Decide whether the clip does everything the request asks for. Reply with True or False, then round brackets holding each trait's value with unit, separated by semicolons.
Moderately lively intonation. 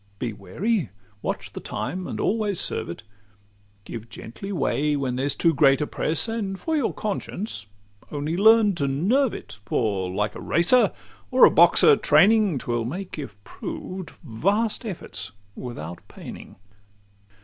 False (9.0 semitones)